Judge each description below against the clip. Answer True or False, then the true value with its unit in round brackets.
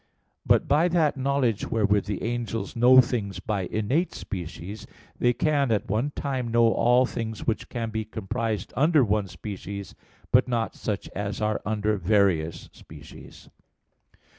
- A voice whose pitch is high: False (110 Hz)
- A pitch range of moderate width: True (3.6 semitones)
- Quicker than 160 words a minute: False (145 wpm)